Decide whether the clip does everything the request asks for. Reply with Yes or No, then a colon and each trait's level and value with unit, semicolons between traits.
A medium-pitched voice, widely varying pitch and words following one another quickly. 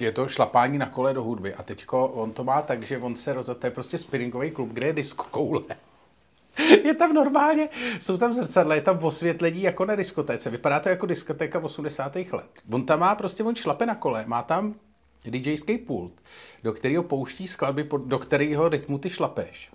Yes: medium, 150 Hz; wide, 6.8 semitones; fast, 200 wpm